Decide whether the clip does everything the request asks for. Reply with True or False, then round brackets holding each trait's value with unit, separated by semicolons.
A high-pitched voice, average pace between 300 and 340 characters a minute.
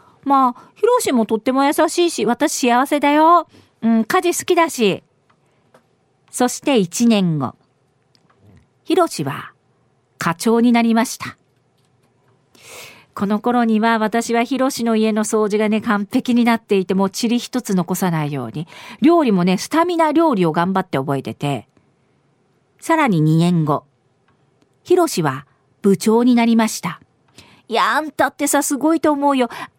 False (225 Hz; 265 characters per minute)